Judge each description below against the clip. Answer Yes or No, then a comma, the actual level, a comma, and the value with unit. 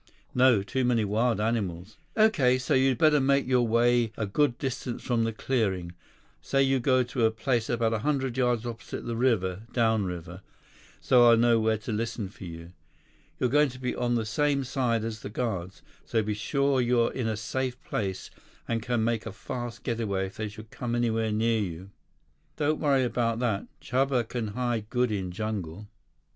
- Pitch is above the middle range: No, low, 115 Hz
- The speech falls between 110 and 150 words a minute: No, average, 180 wpm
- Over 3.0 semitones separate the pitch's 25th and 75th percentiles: No, average, 2.7 semitones